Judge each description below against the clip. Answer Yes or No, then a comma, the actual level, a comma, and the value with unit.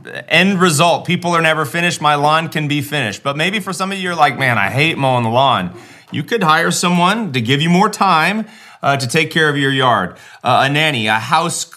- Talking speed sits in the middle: No, fast, 235 wpm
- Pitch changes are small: No, average, 3.8 semitones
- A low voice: No, medium, 155 Hz